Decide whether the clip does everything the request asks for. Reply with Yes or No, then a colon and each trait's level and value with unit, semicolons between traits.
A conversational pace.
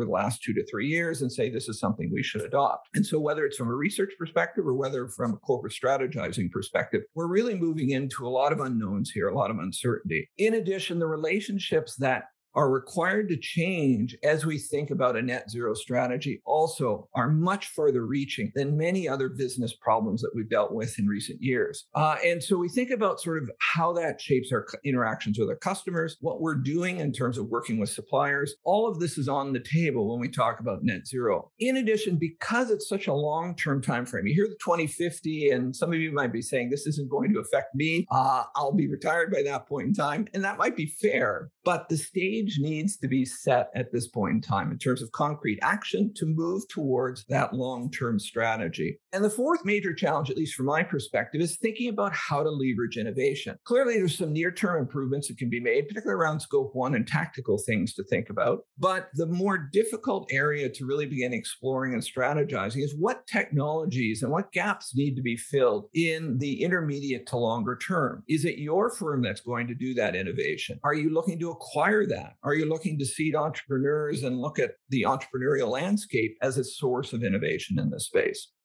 No: fast, 210 wpm